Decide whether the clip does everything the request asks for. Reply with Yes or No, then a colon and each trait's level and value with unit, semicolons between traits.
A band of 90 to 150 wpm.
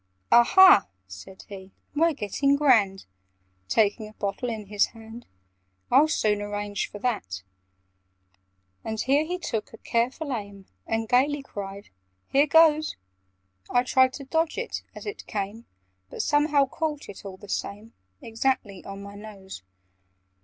Yes: average, 140 wpm